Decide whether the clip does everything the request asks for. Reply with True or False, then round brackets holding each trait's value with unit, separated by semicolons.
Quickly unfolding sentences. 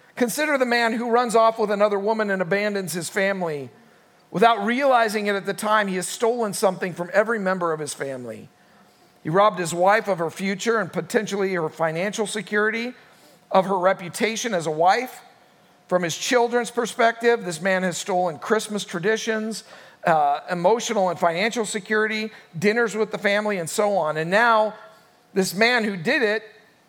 False (170 wpm)